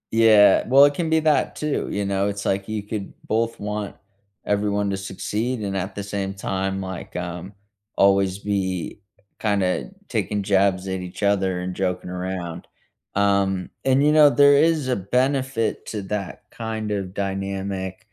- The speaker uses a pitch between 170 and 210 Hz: No, low, 100 Hz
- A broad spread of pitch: No, narrow, 2.4 semitones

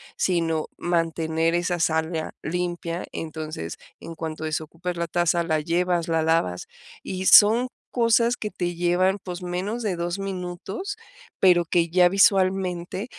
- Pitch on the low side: No, medium, 175 Hz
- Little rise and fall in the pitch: Yes, narrow, 2.1 semitones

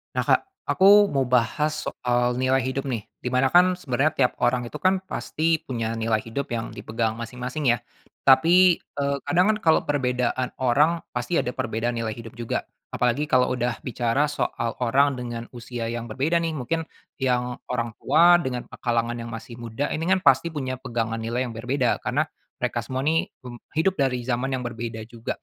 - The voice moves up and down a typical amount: Yes, average, 3.5 semitones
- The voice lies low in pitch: Yes, low, 125 Hz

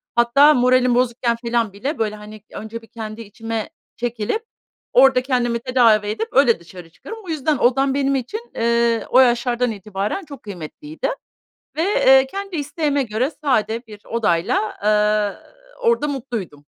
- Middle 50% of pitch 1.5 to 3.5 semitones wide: No, average, 4.0 semitones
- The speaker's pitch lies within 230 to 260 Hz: Yes, high, 240 Hz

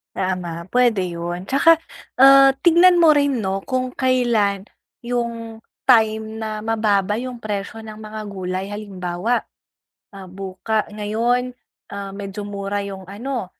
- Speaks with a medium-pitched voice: No, high, 215 Hz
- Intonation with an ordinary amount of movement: Yes, average, 3.9 semitones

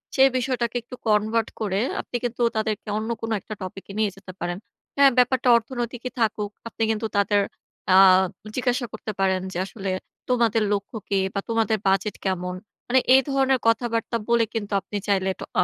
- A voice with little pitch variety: No, average, 3.3 semitones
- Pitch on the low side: No, high, 220 Hz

